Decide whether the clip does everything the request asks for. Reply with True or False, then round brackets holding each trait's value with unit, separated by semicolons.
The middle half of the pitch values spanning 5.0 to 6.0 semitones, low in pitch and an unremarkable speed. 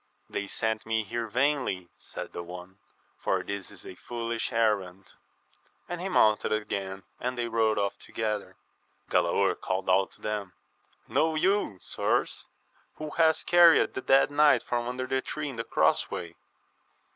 True (5.4 semitones; 110 Hz; 155 wpm)